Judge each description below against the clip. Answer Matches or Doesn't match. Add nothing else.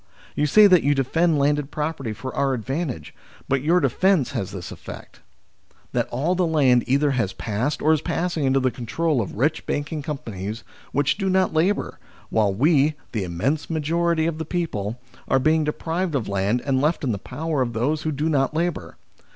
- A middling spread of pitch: Matches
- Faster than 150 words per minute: Matches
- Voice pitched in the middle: Matches